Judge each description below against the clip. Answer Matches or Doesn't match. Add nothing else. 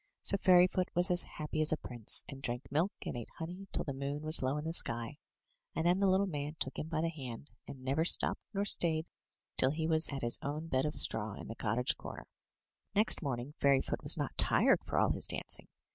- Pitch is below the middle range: Doesn't match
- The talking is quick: Matches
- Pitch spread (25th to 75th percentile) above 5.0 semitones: Doesn't match